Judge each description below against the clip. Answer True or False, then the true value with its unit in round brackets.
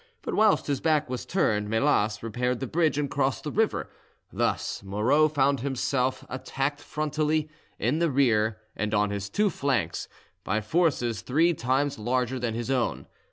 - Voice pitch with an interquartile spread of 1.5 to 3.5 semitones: False (4.7 semitones)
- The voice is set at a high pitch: False (130 Hz)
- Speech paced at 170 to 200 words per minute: False (160 wpm)